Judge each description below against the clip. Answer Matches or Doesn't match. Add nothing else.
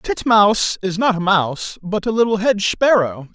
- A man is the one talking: Matches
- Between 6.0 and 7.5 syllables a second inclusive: Doesn't match